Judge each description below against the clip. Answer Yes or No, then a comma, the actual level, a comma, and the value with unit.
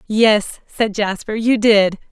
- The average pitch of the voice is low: No, high, 215 Hz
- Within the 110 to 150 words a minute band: Yes, average, 140 wpm